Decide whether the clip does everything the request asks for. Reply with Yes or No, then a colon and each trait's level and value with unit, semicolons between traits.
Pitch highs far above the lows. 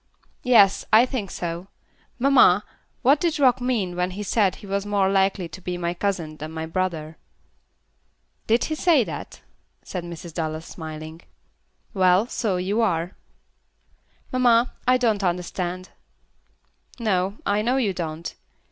No: average, 4.9 semitones